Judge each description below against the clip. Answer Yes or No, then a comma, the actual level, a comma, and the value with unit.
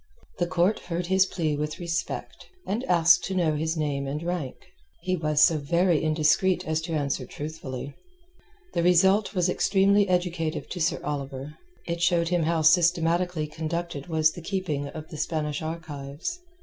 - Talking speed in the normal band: Yes, average, 160 wpm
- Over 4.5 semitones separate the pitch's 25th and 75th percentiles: No, average, 2.7 semitones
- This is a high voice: No, medium, 165 Hz